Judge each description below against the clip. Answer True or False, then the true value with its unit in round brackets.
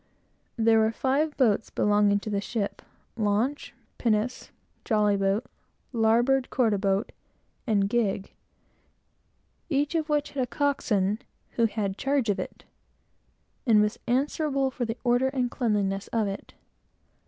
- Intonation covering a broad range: False (4.2 semitones)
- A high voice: True (225 Hz)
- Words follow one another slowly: True (130 wpm)